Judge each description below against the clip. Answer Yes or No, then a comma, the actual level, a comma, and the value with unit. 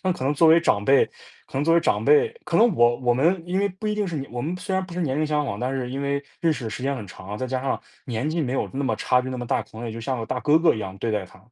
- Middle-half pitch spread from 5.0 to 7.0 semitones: Yes, wide, 5.6 semitones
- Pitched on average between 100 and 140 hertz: Yes, low, 135 Hz